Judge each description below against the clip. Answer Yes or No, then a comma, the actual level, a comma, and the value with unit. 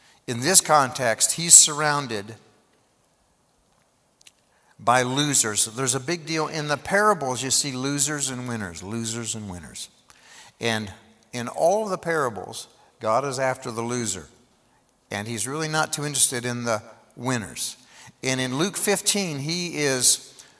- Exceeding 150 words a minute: No, average, 140 wpm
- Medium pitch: No, low, 130 Hz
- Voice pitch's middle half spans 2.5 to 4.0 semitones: No, average, 4.7 semitones